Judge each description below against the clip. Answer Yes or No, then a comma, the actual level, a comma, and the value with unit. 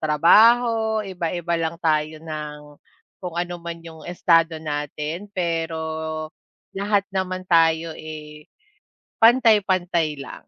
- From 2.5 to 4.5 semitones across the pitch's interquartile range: Yes, average, 3.1 semitones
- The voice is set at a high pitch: No, medium, 170 Hz